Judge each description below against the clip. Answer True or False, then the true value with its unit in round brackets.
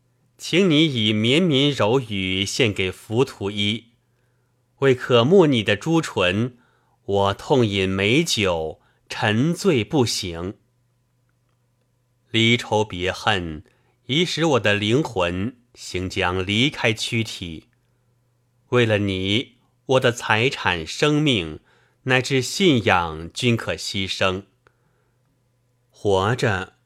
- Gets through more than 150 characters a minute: False (140 characters per minute)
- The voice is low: True (120 Hz)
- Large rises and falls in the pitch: False (3.9 semitones)